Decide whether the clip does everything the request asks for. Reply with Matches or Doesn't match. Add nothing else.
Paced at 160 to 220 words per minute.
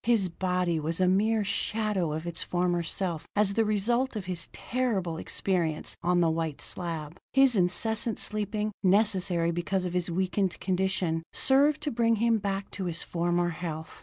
Matches